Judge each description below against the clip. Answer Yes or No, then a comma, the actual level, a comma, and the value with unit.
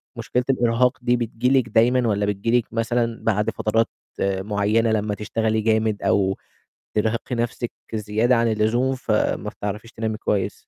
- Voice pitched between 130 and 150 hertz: No, low, 115 Hz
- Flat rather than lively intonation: Yes, narrow, 2.0 semitones